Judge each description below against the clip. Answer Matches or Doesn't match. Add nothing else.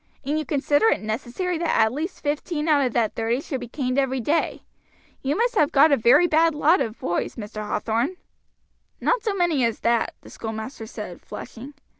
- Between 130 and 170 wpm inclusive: Doesn't match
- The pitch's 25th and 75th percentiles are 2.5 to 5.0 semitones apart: Doesn't match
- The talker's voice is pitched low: Doesn't match